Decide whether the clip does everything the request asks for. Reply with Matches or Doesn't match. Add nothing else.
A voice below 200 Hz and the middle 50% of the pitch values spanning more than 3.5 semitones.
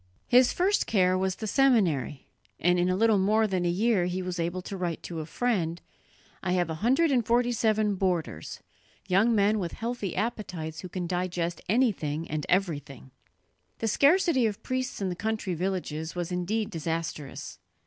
Matches